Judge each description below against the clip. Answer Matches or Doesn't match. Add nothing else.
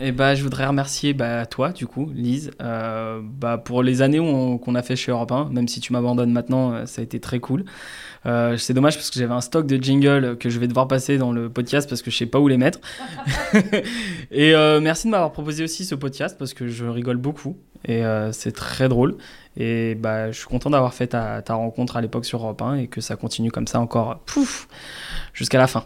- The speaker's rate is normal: Doesn't match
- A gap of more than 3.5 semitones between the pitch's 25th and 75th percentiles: Doesn't match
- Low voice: Matches